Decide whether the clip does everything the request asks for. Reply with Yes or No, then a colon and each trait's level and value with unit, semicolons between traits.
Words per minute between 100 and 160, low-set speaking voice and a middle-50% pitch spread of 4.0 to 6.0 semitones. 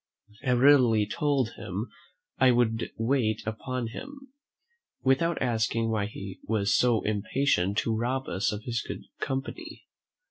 No: slow, 135 wpm; low, 120 Hz; average, 3.4 semitones